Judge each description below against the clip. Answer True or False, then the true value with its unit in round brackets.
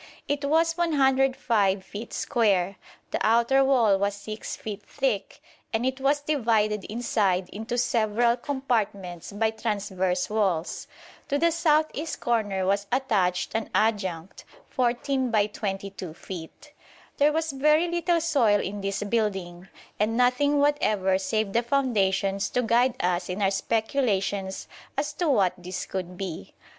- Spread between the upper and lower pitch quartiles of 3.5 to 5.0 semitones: False (5.5 semitones)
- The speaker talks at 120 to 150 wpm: True (140 wpm)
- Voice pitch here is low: False (220 Hz)